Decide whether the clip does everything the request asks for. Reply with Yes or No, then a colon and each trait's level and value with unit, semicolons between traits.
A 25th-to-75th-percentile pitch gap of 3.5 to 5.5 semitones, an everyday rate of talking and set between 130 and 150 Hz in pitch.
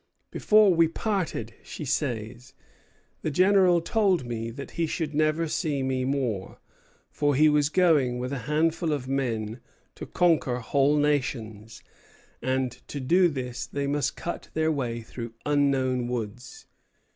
Yes: average, 4.3 semitones; average, 145 wpm; medium, 140 Hz